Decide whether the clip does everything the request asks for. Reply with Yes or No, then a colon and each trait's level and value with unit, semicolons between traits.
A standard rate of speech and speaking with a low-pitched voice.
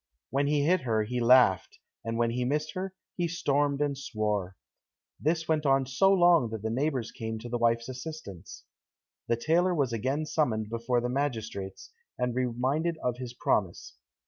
Yes: average, 170 wpm; low, 125 Hz